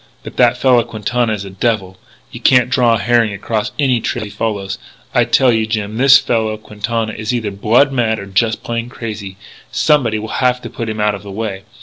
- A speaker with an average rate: No, fast, 215 wpm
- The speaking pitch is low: Yes, low, 110 Hz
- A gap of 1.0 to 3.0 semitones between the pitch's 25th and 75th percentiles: Yes, narrow, 2.4 semitones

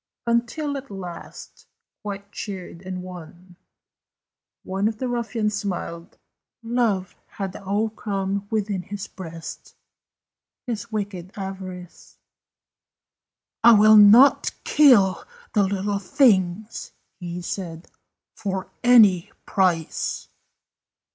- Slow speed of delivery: Yes, slow, 95 wpm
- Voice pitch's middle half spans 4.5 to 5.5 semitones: No, average, 3.0 semitones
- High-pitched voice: Yes, high, 200 Hz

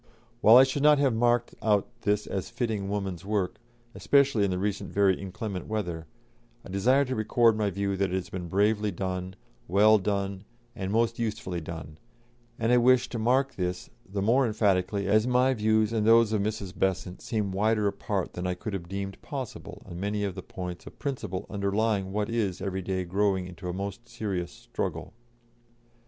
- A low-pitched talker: Yes, low, 100 Hz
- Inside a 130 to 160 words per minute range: No, average, 185 wpm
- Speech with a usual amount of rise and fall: Yes, average, 3.1 semitones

